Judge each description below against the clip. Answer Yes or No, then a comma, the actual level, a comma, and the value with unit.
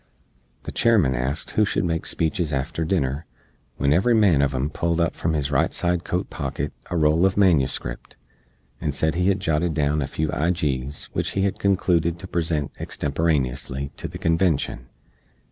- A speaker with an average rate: Yes, average, 170 wpm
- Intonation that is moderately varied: Yes, average, 3.8 semitones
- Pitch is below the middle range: Yes, very low, 80 Hz